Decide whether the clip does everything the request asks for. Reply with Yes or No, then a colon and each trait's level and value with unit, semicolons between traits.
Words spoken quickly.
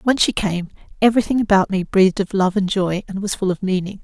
Yes: fast, 240 wpm